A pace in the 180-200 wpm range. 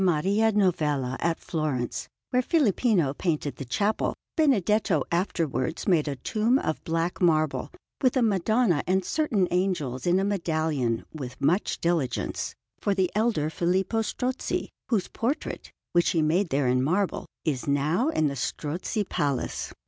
No: average, 145 wpm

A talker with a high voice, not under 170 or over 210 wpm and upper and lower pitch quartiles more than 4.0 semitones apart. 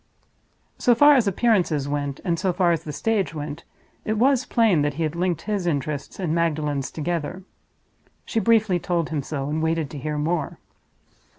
No: medium, 165 Hz; average, 180 wpm; average, 4.9 semitones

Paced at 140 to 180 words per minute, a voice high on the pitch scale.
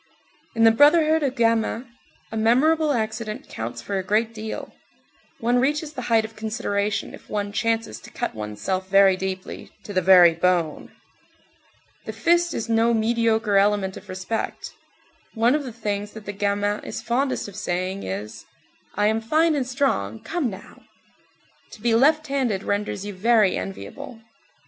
Yes: average, 165 wpm; high, 220 Hz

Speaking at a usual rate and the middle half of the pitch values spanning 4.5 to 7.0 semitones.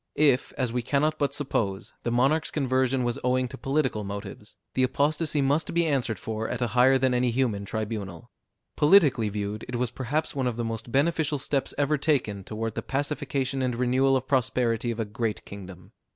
No: average, 190 wpm; average, 3.7 semitones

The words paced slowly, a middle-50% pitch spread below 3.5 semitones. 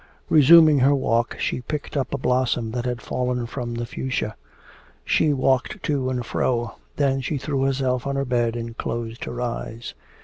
No: average, 175 wpm; narrow, 2.6 semitones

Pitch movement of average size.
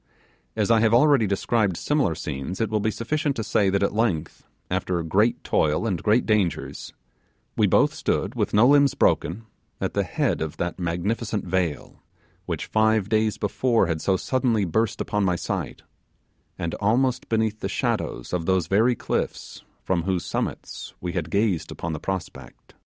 Yes: average, 4.3 semitones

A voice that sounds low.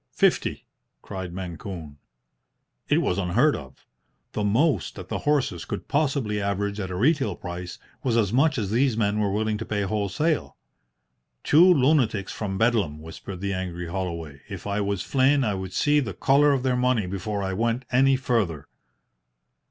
Yes: low, 105 Hz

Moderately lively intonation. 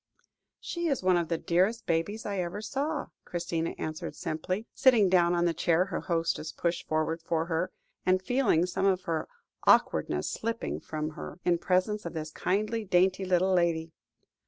Yes: average, 3.5 semitones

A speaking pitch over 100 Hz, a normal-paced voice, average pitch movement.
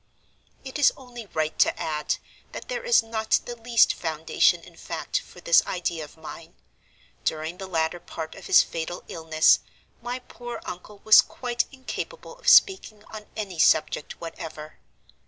No: high, 190 Hz; average, 155 wpm; wide, 7.0 semitones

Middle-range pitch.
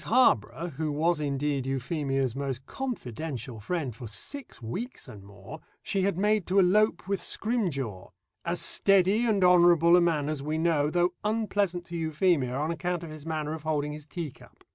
Yes: medium, 160 Hz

